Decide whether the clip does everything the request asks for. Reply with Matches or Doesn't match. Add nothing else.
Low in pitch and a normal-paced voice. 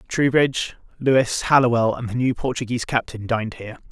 Matches